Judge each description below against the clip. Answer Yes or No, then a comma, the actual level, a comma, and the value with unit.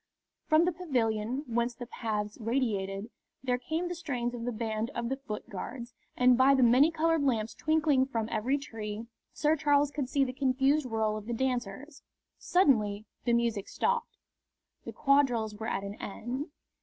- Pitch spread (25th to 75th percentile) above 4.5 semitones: No, average, 4.2 semitones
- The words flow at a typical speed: Yes, average, 170 wpm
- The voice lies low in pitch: No, high, 245 Hz